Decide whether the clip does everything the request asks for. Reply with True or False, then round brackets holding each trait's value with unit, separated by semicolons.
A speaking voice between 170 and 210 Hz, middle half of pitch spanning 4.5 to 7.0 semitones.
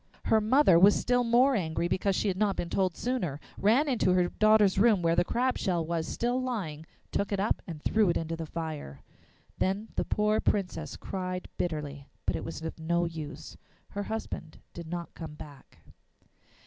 True (185 Hz; 4.8 semitones)